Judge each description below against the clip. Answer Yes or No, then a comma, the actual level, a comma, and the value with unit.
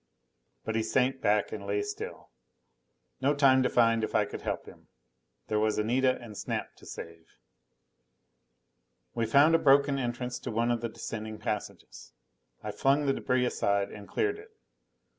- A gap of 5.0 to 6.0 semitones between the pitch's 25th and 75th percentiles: No, average, 4.0 semitones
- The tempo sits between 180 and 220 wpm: No, average, 165 wpm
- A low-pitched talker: Yes, low, 120 Hz